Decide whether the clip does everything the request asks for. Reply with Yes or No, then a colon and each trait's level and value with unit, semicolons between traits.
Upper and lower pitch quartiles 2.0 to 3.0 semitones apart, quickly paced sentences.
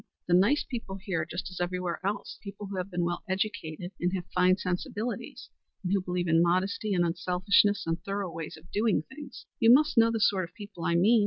Yes: average, 2.7 semitones; fast, 220 wpm